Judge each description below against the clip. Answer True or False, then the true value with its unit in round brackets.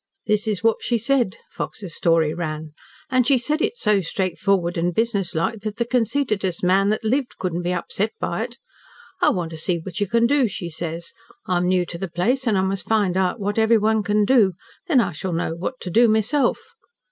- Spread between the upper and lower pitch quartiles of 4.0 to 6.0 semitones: True (4.6 semitones)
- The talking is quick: True (215 wpm)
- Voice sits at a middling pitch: False (200 Hz)